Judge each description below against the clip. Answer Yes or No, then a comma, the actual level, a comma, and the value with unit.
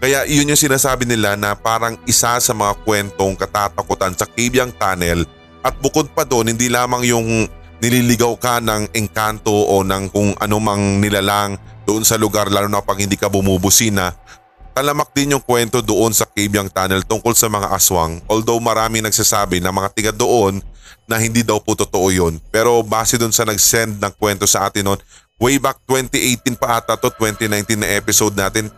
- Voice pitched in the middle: No, low, 110 Hz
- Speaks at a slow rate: No, average, 175 wpm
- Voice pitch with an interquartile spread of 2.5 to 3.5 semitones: Yes, average, 2.9 semitones